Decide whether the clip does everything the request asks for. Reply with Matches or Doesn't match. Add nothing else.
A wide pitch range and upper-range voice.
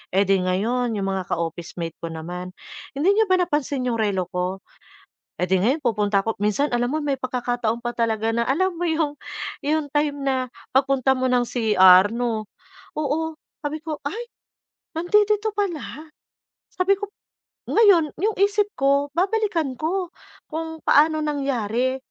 Matches